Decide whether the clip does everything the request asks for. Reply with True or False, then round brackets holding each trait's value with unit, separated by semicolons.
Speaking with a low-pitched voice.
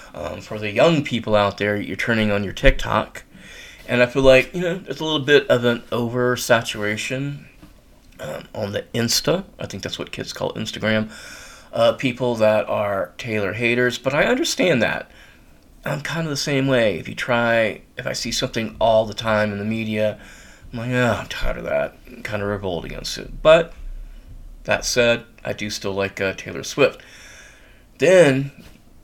True (115 Hz)